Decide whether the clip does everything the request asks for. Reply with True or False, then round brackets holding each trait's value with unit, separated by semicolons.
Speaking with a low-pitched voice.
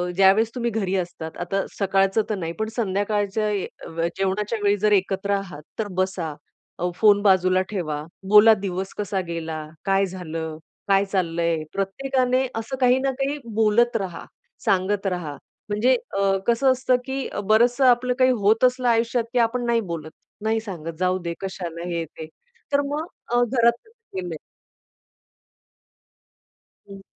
False (200 Hz)